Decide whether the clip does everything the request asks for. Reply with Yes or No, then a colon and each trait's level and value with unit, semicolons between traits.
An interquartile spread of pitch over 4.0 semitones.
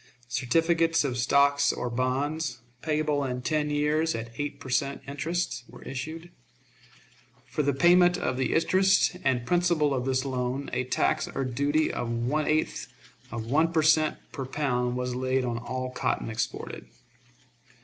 No: average, 3.7 semitones